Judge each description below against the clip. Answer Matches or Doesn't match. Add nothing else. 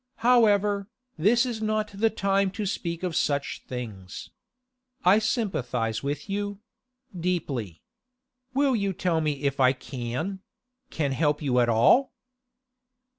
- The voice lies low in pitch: Doesn't match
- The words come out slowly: Matches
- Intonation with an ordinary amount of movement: Doesn't match